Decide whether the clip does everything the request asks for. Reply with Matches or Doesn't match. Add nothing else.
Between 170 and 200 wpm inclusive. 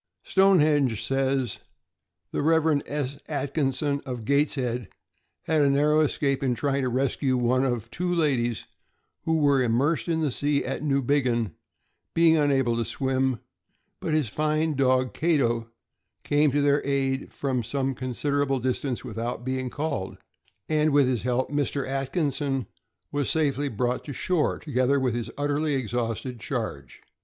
Doesn't match